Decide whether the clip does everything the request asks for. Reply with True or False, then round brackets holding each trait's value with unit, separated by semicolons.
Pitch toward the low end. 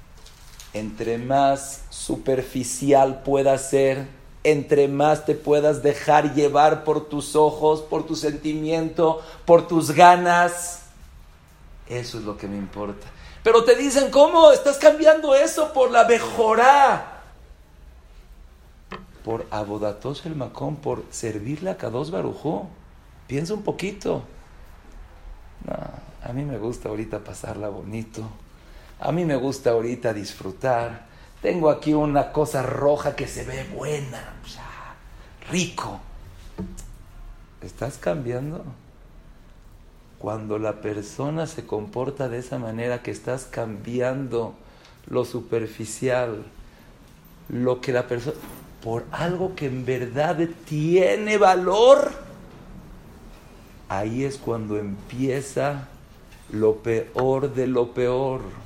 True (130 Hz)